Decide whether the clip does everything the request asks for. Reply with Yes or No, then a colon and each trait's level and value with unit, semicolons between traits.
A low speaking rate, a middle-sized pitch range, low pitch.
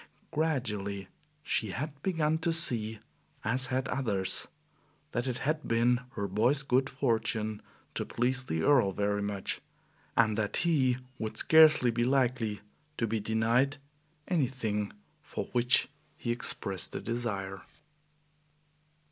Yes: slow, 125 wpm; average, 4.3 semitones; low, 120 Hz